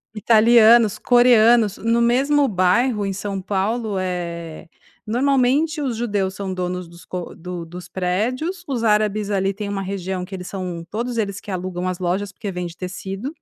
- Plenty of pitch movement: No, average, 4.3 semitones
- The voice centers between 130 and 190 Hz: No, high, 200 Hz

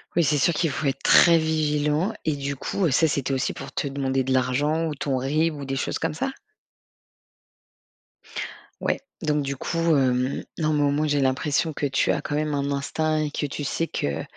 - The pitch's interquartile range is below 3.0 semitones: Yes, narrow, 2.4 semitones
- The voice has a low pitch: No, medium, 145 Hz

